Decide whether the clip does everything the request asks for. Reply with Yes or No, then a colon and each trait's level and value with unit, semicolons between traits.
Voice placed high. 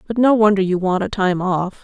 Yes: high, 195 Hz